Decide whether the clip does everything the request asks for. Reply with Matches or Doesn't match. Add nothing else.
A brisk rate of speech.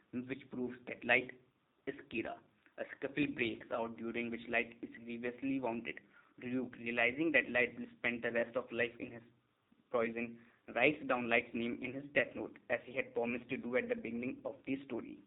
Doesn't match